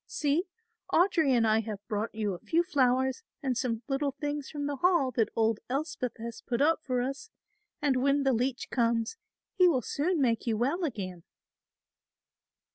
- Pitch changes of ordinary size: Yes, average, 4.1 semitones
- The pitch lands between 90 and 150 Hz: No, very high, 260 Hz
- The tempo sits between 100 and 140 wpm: No, average, 175 wpm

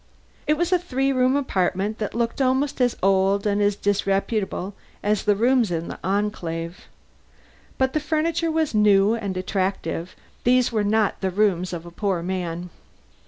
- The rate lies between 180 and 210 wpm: No, average, 165 wpm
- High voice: Yes, high, 205 Hz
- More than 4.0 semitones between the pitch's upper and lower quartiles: Yes, average, 5.1 semitones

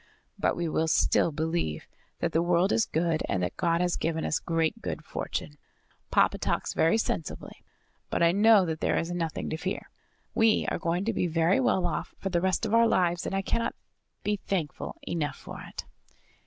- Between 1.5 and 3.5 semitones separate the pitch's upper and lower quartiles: Yes, average, 3.1 semitones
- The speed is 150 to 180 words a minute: No, average, 195 wpm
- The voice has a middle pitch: Yes, medium, 170 Hz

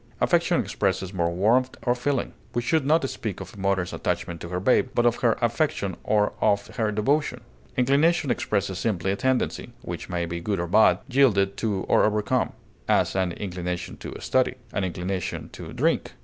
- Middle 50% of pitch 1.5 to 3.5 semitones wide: No, average, 4.8 semitones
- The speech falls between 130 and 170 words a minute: No, average, 180 wpm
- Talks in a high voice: No, low, 100 Hz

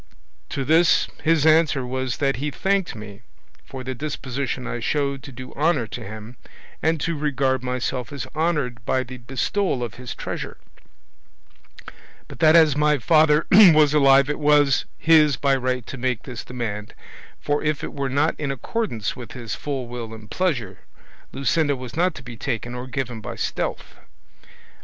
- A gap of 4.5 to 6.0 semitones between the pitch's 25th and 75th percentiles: No, average, 3.5 semitones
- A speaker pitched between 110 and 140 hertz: Yes, low, 135 Hz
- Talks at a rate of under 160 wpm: No, average, 170 wpm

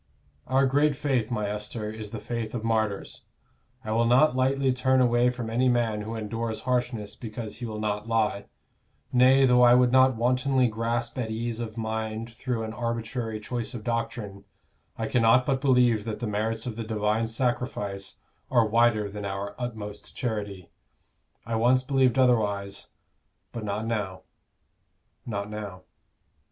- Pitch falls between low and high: No, low, 115 Hz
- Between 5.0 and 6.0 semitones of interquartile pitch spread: No, narrow, 2.6 semitones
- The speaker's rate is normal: Yes, average, 160 wpm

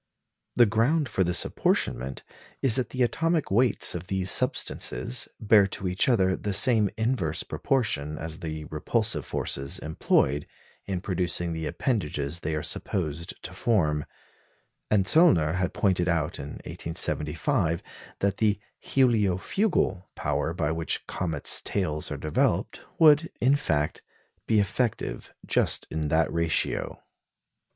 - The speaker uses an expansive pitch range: Yes, wide, 6.2 semitones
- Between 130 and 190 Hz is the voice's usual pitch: No, very low, 90 Hz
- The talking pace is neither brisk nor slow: No, slow, 130 wpm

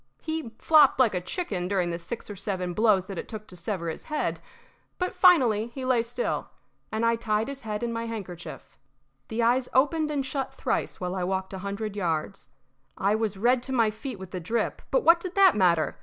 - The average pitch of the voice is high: Yes, high, 220 Hz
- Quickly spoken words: Yes, fast, 215 wpm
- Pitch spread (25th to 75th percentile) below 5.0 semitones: No, wide, 5.4 semitones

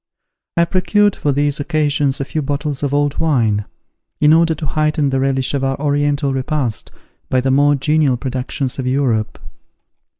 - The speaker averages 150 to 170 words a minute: Yes, average, 165 wpm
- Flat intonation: Yes, narrow, 2.3 semitones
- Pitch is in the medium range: Yes, medium, 145 Hz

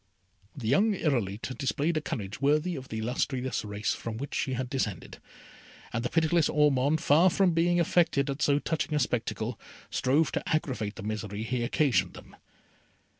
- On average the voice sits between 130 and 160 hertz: Yes, low, 135 Hz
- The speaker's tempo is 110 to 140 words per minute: No, average, 170 wpm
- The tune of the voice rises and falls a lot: No, average, 5.0 semitones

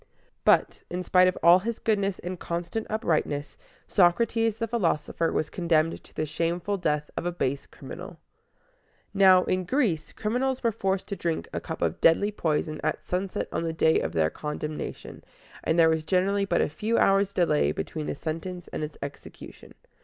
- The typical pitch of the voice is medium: Yes, medium, 175 Hz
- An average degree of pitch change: Yes, average, 4.0 semitones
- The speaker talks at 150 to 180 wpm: Yes, average, 175 wpm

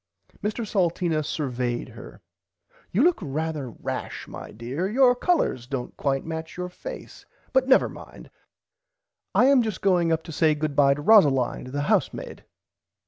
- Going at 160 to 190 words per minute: No, average, 145 wpm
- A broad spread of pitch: Yes, wide, 7.3 semitones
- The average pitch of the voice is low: No, medium, 160 Hz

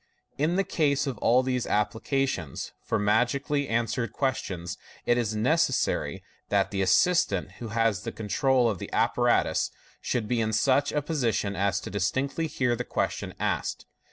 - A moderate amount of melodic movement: Yes, average, 4.9 semitones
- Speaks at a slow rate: No, average, 165 wpm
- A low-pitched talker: Yes, low, 120 Hz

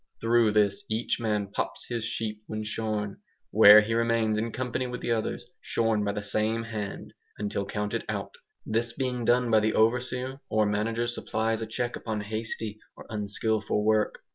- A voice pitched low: Yes, low, 110 Hz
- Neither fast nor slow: Yes, average, 170 wpm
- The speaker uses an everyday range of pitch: No, narrow, 1.6 semitones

